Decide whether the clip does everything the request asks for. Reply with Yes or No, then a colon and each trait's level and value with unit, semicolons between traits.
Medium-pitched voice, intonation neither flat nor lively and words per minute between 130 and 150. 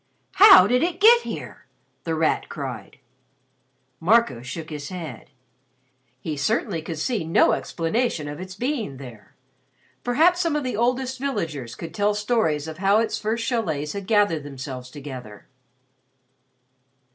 No: medium, 180 Hz; wide, 8.5 semitones; average, 140 wpm